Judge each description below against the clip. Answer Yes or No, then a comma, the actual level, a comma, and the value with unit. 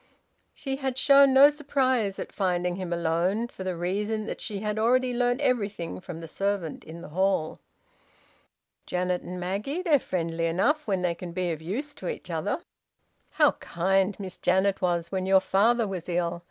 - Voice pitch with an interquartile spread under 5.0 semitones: No, average, 5.3 semitones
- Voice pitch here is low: No, high, 190 Hz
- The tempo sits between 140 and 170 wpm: No, average, 180 wpm